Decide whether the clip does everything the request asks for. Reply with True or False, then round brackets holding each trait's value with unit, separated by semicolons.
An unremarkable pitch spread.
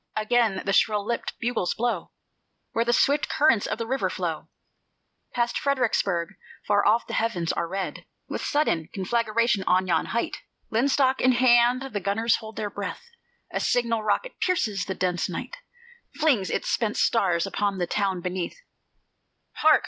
True (4.0 semitones)